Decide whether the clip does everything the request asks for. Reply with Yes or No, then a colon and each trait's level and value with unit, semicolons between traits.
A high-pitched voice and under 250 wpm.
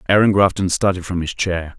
No: very low, 90 Hz; average, 200 wpm